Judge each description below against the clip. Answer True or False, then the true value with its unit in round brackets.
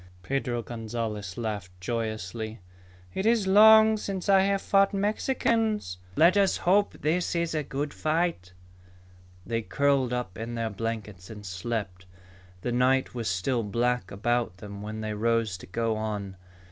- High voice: False (115 Hz)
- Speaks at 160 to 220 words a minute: False (145 wpm)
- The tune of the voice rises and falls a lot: True (8.2 semitones)